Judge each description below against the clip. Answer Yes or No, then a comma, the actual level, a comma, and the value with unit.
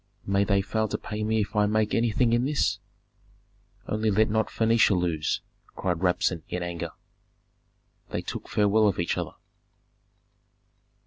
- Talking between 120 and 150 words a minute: Yes, average, 145 wpm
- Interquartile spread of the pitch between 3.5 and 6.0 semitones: No, average, 2.9 semitones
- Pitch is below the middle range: Yes, low, 105 Hz